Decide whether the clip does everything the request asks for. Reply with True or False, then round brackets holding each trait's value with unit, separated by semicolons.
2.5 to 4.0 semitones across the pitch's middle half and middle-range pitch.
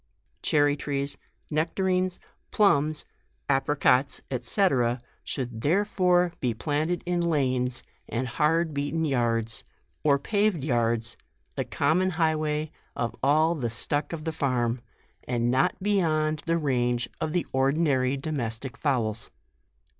False (4.4 semitones; 145 Hz)